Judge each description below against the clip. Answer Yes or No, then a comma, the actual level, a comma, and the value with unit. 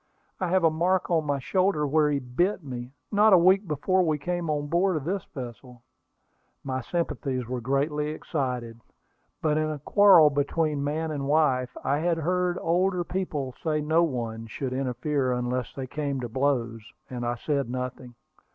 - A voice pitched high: No, medium, 150 Hz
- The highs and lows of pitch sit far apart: No, average, 4.8 semitones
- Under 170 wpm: No, average, 175 wpm